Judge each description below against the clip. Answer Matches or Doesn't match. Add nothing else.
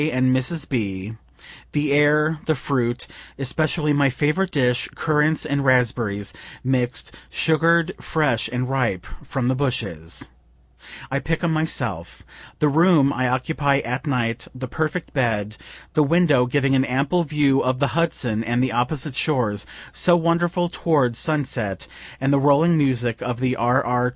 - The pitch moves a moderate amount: Matches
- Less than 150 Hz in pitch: Matches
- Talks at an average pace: Matches